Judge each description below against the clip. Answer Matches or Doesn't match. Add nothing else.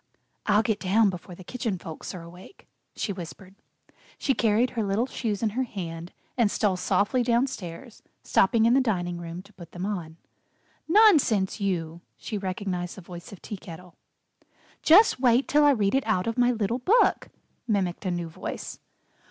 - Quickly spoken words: Doesn't match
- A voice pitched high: Matches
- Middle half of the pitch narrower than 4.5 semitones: Doesn't match